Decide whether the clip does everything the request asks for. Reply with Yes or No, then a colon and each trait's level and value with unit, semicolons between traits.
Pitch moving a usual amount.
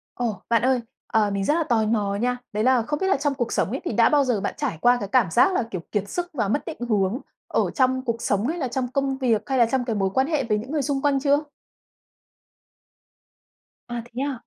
Yes: average, 3.9 semitones